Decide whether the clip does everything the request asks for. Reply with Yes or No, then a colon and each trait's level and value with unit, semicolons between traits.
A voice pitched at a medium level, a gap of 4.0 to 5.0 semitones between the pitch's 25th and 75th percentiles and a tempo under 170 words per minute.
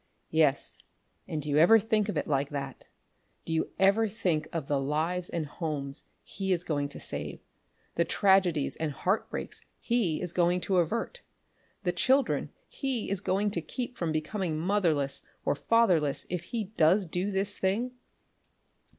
Yes: medium, 175 Hz; average, 4.7 semitones; average, 160 wpm